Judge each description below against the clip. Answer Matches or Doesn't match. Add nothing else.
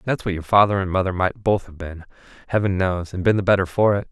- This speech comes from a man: Matches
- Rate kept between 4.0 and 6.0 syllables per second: Doesn't match